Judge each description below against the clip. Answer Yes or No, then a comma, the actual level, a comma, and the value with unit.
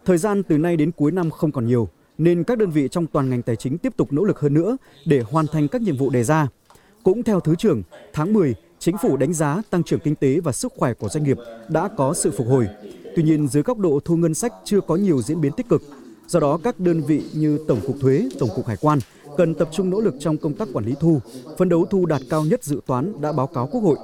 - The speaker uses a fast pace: Yes, fast, 275 wpm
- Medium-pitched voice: Yes, medium, 155 Hz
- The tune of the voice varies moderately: Yes, average, 4.7 semitones